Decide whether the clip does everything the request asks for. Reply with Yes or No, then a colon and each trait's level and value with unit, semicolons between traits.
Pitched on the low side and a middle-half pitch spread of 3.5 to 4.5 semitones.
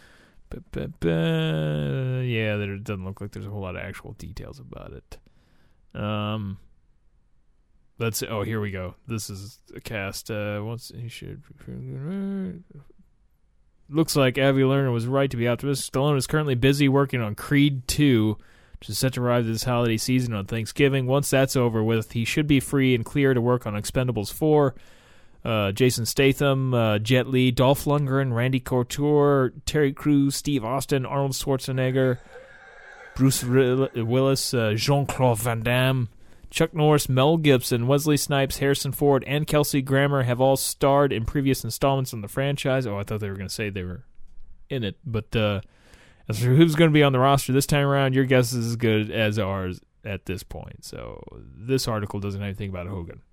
Yes: low, 125 Hz; average, 4.2 semitones